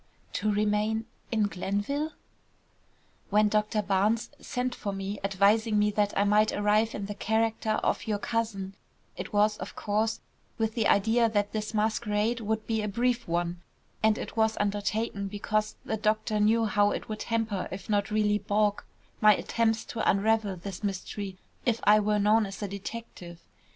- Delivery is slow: No, average, 165 wpm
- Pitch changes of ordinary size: No, narrow, 1.5 semitones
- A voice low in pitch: No, high, 210 Hz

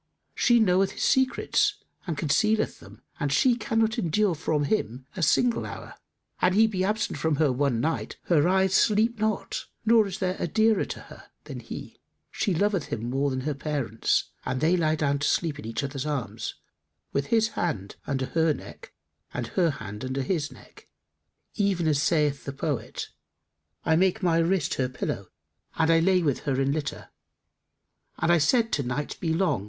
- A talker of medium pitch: Yes, medium, 160 Hz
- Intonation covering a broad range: Yes, wide, 5.7 semitones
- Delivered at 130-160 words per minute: No, average, 185 wpm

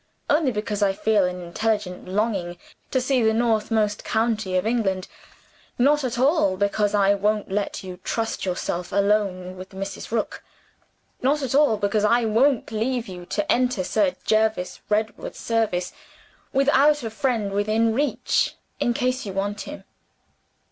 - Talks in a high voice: Yes, high, 215 Hz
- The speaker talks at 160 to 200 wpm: No, average, 150 wpm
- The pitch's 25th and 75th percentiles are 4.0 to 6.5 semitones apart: No, average, 3.4 semitones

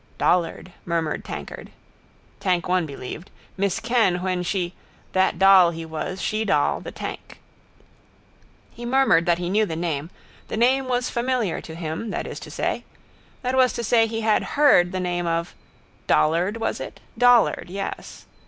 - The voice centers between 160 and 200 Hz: Yes, medium, 185 Hz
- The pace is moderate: Yes, average, 160 wpm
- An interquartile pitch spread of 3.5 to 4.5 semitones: No, average, 5.1 semitones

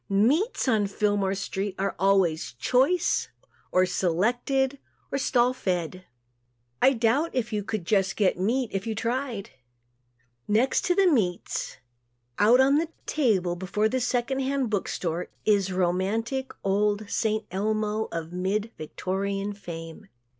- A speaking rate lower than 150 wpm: Yes, slow, 135 wpm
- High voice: Yes, high, 210 Hz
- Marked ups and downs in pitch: No, average, 4.6 semitones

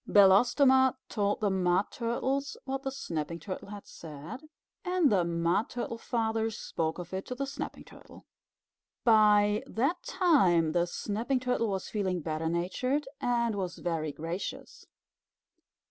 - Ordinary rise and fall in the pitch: No, wide, 6.2 semitones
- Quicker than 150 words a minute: No, average, 140 wpm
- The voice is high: Yes, high, 210 Hz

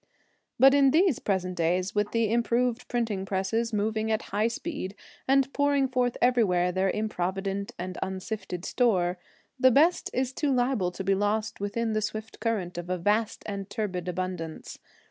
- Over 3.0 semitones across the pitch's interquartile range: Yes, average, 4.5 semitones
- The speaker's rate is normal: Yes, average, 165 wpm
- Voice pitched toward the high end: Yes, high, 210 Hz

